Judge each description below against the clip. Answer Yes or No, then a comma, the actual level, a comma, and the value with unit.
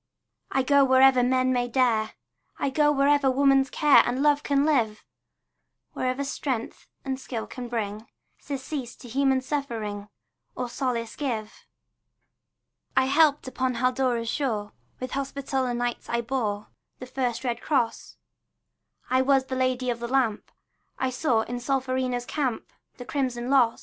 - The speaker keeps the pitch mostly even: Yes, narrow, 2.2 semitones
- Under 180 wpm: Yes, average, 145 wpm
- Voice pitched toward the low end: No, very high, 255 Hz